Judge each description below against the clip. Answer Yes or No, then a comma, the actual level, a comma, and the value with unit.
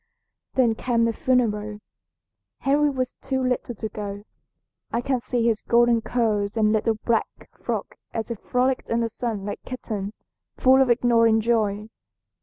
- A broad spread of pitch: No, narrow, 2.6 semitones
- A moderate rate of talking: Yes, average, 160 wpm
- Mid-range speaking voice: No, high, 230 Hz